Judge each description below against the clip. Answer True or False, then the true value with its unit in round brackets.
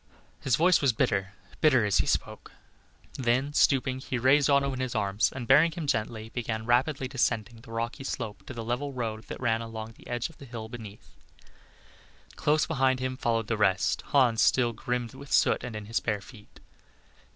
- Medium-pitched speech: False (120 Hz)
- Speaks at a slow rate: False (190 wpm)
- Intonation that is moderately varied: True (3.0 semitones)